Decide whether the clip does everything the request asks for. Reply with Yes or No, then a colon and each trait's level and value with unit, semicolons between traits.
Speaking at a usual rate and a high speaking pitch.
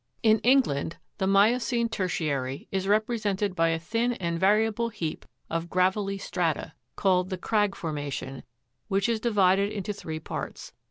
Yes: average, 155 wpm; high, 195 Hz